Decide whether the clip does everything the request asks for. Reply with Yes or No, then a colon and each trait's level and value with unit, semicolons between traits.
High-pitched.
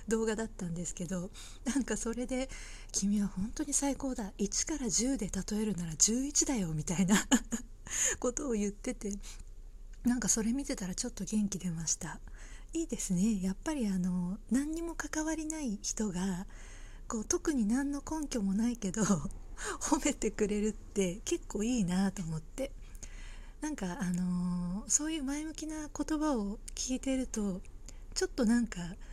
Yes: high, 225 Hz